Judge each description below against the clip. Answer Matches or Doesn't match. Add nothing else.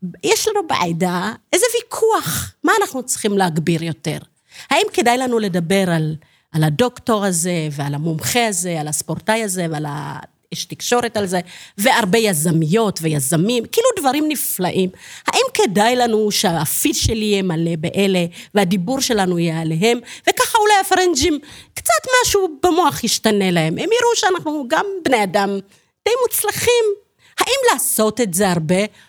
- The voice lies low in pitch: Doesn't match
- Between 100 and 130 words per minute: Doesn't match